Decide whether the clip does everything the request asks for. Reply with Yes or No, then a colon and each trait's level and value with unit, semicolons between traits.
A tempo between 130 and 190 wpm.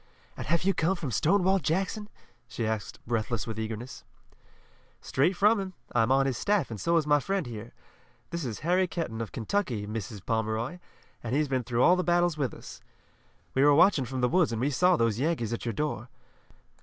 No: average, 200 wpm